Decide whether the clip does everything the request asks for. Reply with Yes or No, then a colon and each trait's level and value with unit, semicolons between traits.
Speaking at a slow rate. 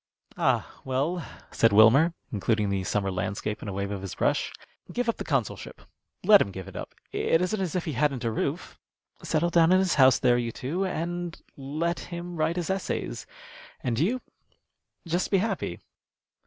No: average, 180 wpm